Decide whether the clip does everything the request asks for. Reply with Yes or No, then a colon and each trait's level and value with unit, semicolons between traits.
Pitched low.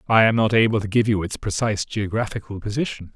Yes: low, 105 Hz